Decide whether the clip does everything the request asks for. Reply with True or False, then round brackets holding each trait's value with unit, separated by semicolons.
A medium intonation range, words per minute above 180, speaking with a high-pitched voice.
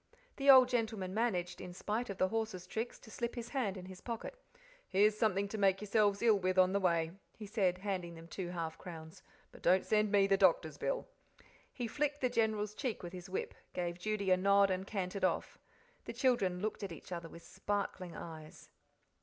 True (3.3 semitones; 205 wpm; 200 Hz)